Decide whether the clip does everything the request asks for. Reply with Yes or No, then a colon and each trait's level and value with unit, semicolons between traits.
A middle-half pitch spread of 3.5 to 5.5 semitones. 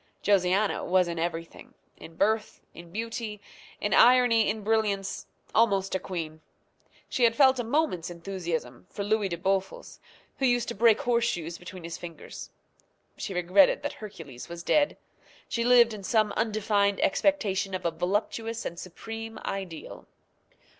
Yes: average, 4.2 semitones